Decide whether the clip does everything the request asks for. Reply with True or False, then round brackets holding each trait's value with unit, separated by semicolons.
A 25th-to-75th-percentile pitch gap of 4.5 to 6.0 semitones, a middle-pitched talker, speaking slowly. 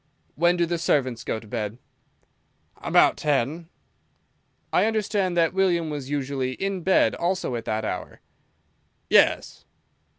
True (5.6 semitones; 160 Hz; 130 wpm)